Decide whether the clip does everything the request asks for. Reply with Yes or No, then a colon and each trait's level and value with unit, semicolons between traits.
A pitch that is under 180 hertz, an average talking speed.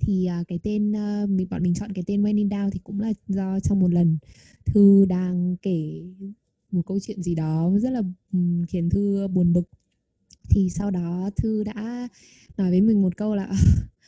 No: high, 190 Hz; average, 185 wpm